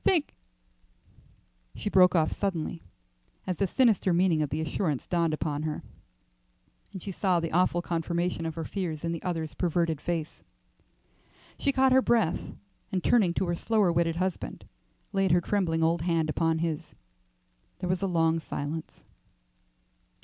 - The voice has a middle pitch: Yes, medium, 170 Hz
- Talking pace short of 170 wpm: Yes, average, 155 wpm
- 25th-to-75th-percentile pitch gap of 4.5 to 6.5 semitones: No, narrow, 2.5 semitones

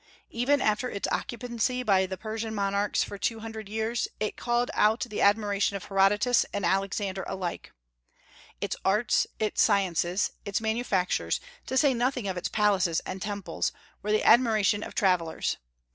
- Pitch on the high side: Yes, high, 210 Hz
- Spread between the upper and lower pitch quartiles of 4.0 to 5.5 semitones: No, average, 2.7 semitones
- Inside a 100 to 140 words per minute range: No, average, 155 wpm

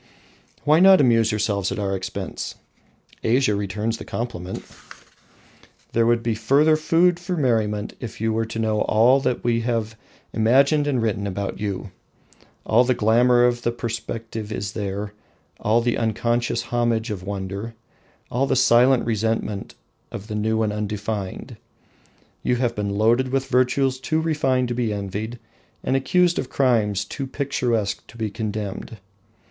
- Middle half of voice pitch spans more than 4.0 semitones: No, average, 3.1 semitones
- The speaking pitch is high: No, low, 115 Hz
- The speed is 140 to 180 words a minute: Yes, average, 155 wpm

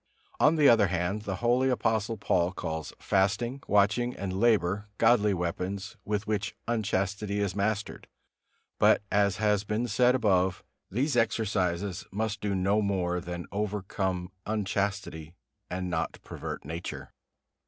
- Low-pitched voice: Yes, low, 100 Hz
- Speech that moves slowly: Yes, slow, 130 wpm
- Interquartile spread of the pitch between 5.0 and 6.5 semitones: No, average, 2.7 semitones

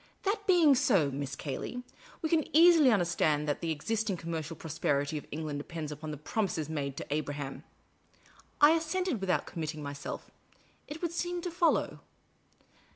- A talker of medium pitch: Yes, medium, 165 Hz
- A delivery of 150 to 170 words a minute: Yes, average, 160 wpm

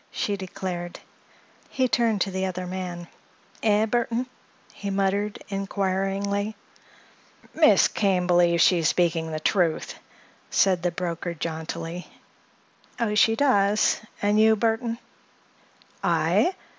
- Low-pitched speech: No, high, 195 Hz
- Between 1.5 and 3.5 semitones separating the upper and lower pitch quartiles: Yes, average, 3.1 semitones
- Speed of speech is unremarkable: No, slow, 115 wpm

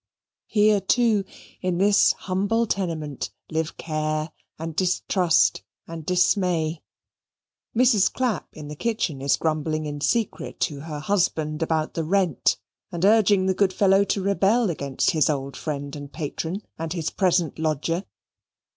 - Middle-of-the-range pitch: Yes, medium, 170 Hz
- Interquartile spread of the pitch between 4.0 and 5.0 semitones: Yes, average, 4.3 semitones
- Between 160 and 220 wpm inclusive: No, average, 140 wpm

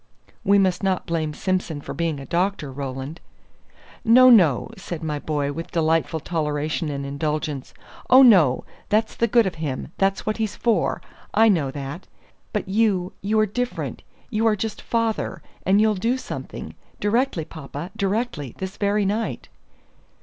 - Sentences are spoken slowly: No, average, 155 wpm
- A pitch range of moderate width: No, wide, 6.0 semitones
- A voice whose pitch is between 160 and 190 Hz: Yes, medium, 185 Hz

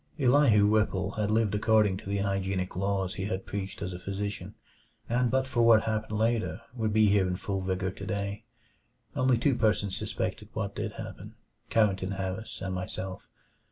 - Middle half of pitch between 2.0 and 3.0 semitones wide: Yes, narrow, 2.4 semitones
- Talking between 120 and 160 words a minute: No, average, 170 wpm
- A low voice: Yes, low, 100 Hz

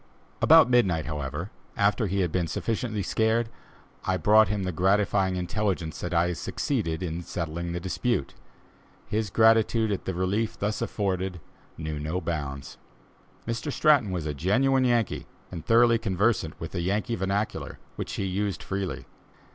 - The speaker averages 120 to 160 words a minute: Yes, average, 155 wpm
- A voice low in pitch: Yes, very low, 95 Hz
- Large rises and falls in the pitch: No, average, 4.3 semitones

